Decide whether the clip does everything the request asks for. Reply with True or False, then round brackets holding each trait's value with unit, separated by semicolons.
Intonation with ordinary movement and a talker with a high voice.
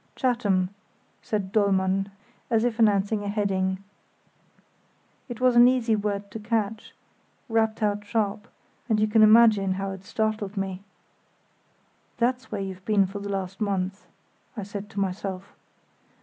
False (2.3 semitones; 205 Hz)